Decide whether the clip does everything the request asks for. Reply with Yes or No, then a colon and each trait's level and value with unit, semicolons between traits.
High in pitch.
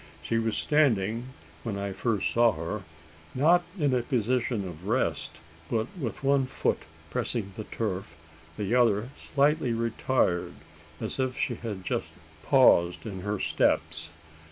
No: low, 115 Hz